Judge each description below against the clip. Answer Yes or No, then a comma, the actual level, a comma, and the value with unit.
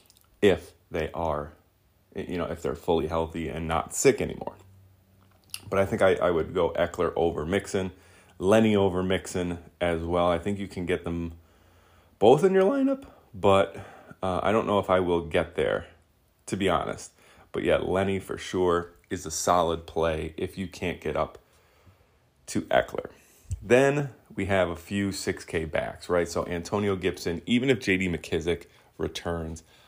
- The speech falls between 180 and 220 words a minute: No, average, 165 wpm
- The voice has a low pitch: Yes, very low, 90 Hz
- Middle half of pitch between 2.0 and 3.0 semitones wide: Yes, narrow, 2.4 semitones